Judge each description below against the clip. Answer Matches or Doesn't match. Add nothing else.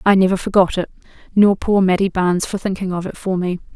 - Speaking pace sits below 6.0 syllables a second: Doesn't match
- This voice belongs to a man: Doesn't match